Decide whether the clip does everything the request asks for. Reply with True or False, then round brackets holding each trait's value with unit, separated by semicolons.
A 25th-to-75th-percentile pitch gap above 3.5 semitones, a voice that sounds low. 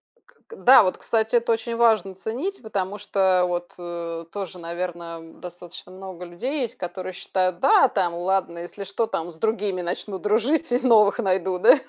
False (3.9 semitones; 190 Hz)